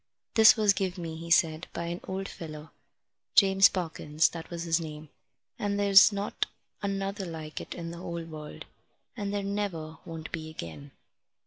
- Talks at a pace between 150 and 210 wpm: Yes, average, 165 wpm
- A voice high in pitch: No, medium, 170 Hz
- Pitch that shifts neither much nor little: Yes, average, 3.7 semitones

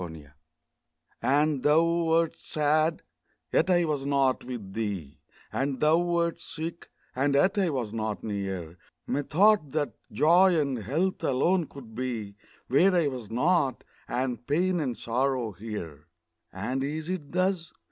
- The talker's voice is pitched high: No, medium, 140 Hz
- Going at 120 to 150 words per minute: Yes, slow, 135 wpm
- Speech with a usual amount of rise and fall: No, wide, 6.0 semitones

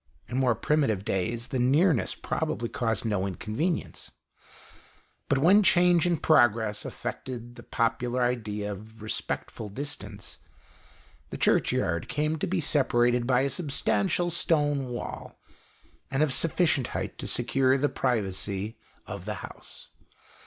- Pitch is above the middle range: No, low, 125 Hz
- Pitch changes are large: No, average, 4.9 semitones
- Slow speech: Yes, slow, 125 wpm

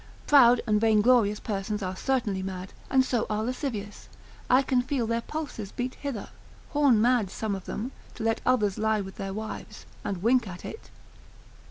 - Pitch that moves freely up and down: No, average, 3.7 semitones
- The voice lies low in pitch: No, high, 220 Hz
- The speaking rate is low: No, average, 175 wpm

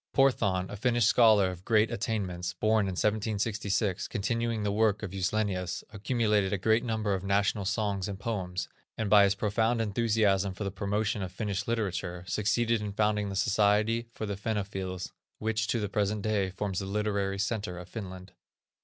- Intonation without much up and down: Yes, narrow, 2.2 semitones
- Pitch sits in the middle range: No, low, 105 Hz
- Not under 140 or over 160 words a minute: No, average, 170 wpm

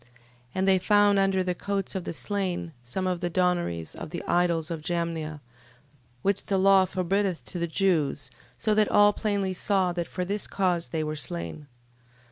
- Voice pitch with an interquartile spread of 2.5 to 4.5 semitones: Yes, average, 2.8 semitones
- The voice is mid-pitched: Yes, medium, 180 Hz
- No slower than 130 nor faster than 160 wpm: No, average, 180 wpm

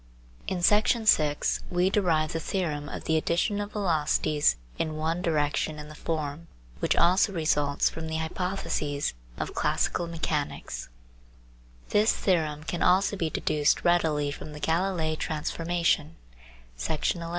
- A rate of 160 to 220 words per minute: No, average, 140 wpm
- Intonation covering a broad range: No, average, 2.7 semitones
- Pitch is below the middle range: No, medium, 160 Hz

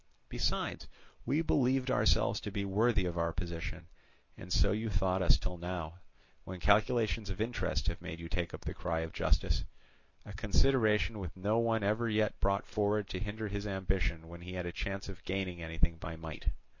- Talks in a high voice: No, very low, 95 Hz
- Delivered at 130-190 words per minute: Yes, average, 185 wpm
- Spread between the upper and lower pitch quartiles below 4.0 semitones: Yes, average, 3.6 semitones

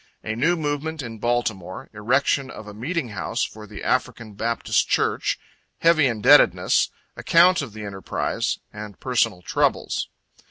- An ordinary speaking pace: No, slow, 130 wpm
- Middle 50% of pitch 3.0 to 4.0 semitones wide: No, wide, 5.5 semitones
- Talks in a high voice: No, low, 115 Hz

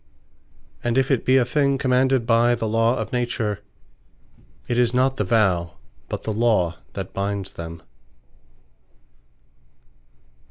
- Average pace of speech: No, slow, 130 wpm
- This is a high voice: No, low, 115 Hz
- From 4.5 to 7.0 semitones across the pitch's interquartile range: No, average, 3.7 semitones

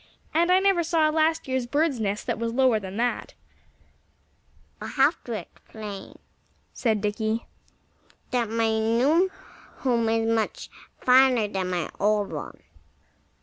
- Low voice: No, high, 230 Hz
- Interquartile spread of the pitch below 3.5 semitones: No, average, 4.4 semitones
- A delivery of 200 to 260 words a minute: No, average, 145 wpm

